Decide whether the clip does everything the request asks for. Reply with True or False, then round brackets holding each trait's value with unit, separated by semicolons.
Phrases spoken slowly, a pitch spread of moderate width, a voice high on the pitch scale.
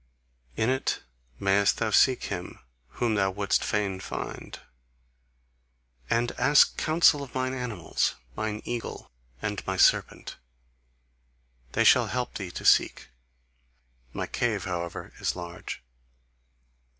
False (115 wpm; 4.3 semitones; 105 Hz)